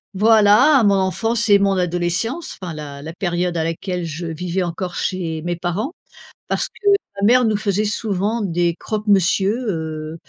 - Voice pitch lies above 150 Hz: Yes, medium, 185 Hz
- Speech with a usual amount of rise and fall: Yes, average, 3.7 semitones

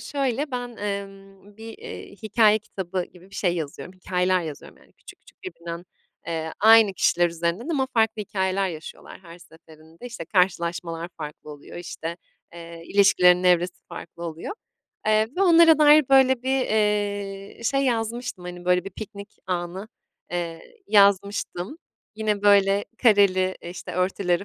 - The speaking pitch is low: No, high, 195 Hz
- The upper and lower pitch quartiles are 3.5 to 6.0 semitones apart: Yes, average, 3.9 semitones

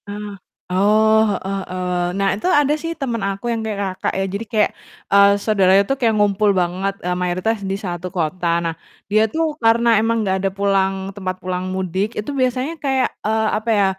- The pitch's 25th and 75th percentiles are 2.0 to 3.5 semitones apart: Yes, average, 3.0 semitones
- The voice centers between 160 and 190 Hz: No, high, 200 Hz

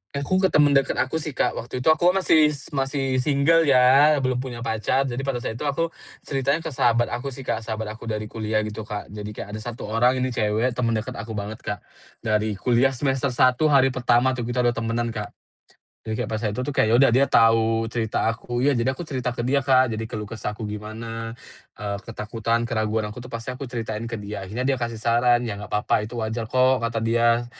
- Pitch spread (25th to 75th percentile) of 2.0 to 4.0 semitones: Yes, average, 2.9 semitones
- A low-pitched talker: Yes, low, 120 Hz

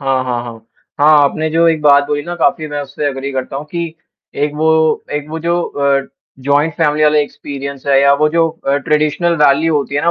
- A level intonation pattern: Yes, narrow, 2.0 semitones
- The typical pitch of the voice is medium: Yes, medium, 145 Hz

